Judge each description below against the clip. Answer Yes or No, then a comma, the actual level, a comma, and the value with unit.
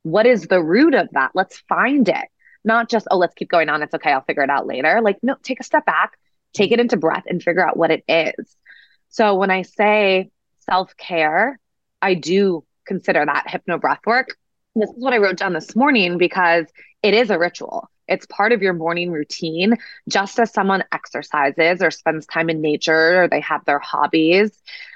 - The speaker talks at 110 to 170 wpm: No, fast, 205 wpm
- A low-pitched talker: No, medium, 185 Hz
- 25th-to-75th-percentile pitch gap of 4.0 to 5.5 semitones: Yes, average, 4.6 semitones